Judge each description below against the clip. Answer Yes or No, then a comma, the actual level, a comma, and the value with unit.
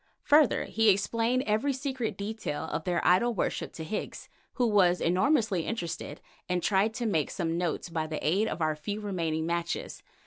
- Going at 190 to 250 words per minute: No, average, 175 wpm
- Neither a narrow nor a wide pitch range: Yes, average, 4.9 semitones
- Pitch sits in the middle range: No, high, 195 Hz